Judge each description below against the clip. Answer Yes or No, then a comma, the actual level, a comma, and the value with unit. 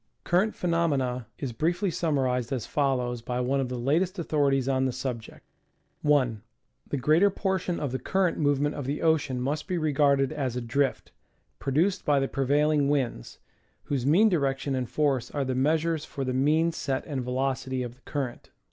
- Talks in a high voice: No, medium, 140 Hz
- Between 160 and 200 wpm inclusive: Yes, average, 175 wpm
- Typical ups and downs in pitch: Yes, average, 3.2 semitones